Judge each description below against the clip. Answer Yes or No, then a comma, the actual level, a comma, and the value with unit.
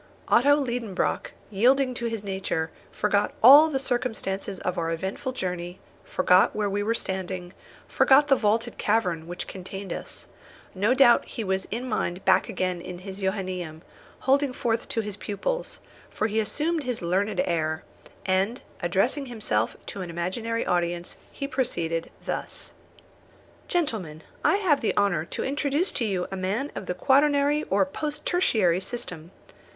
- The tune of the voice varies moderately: No, wide, 5.8 semitones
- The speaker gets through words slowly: No, average, 155 wpm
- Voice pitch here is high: Yes, high, 205 Hz